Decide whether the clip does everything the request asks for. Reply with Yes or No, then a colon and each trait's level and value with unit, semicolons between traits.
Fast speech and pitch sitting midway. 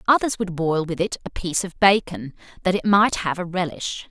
Yes: fast, 220 wpm; medium, 180 Hz